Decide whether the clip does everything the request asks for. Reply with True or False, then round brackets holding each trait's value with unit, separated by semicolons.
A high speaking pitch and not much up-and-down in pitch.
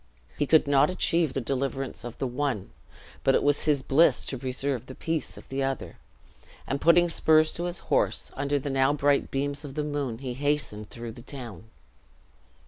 False (140 Hz; 2.1 semitones)